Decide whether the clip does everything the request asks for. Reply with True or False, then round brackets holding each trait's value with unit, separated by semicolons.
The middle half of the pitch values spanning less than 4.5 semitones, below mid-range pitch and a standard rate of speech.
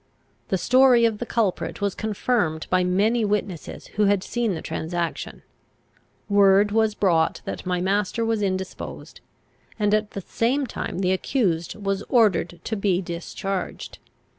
False (3.2 semitones; 200 Hz; 145 wpm)